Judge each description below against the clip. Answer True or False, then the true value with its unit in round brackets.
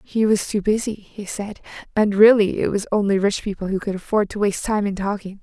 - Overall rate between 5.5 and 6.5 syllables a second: True (5.7 syllables/s)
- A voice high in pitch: True (205 Hz)